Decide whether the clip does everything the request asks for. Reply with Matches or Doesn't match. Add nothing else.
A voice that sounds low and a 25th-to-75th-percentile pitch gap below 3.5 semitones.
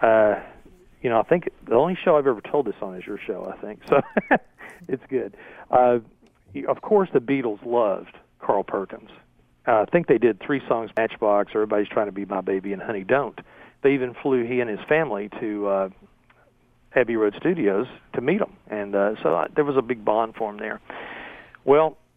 Doesn't match